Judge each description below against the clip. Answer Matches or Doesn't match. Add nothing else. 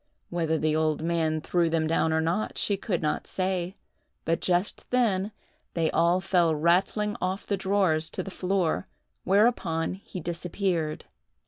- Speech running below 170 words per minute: Matches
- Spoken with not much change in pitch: Doesn't match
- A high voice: Doesn't match